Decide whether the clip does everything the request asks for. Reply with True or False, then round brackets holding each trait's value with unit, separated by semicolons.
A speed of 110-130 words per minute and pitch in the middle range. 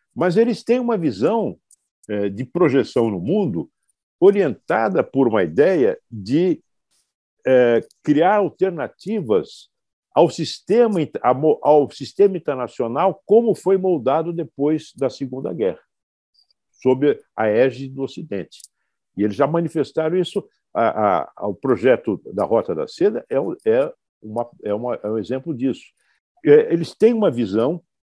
True (125 wpm; 160 Hz)